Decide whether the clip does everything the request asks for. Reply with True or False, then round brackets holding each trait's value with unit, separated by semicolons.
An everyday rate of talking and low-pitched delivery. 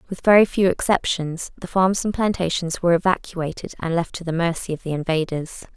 False (190 wpm; 175 Hz)